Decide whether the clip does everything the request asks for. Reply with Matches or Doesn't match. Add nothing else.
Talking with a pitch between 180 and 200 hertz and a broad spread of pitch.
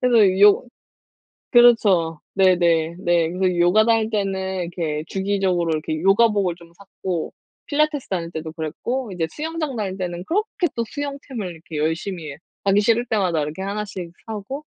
Doesn't match